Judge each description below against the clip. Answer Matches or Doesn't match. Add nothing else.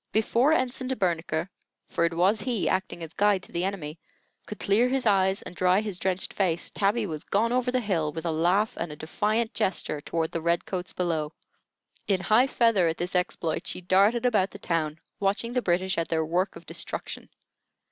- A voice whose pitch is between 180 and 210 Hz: Matches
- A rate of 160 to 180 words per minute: Doesn't match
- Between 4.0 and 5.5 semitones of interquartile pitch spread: Matches